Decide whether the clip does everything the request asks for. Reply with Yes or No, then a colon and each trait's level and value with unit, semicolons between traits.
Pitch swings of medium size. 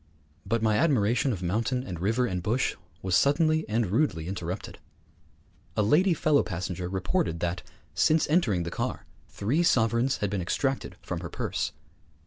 No: wide, 6.7 semitones